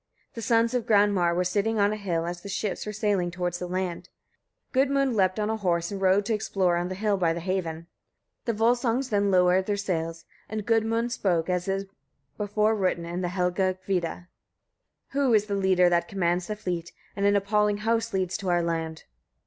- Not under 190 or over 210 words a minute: Yes, average, 195 wpm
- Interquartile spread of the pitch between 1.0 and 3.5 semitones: Yes, average, 3.2 semitones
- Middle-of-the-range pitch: No, high, 195 Hz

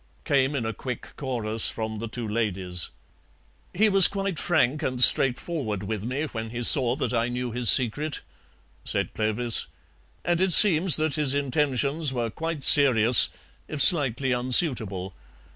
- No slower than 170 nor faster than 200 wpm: No, average, 150 wpm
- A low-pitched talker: Yes, low, 125 Hz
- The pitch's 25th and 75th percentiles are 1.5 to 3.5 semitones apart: No, average, 4.8 semitones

